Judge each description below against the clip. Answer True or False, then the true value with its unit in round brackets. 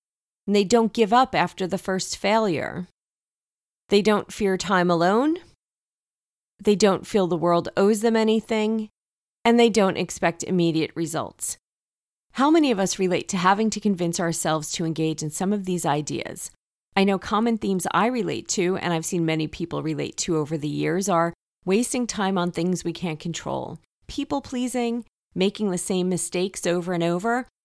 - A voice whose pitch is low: False (190 Hz)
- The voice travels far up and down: False (3.9 semitones)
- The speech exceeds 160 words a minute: True (170 wpm)